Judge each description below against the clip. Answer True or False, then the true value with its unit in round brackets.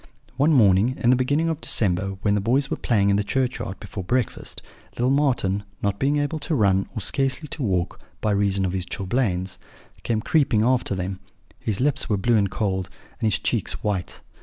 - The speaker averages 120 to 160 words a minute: False (195 wpm)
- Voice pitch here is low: True (110 Hz)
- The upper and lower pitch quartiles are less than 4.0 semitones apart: False (5.2 semitones)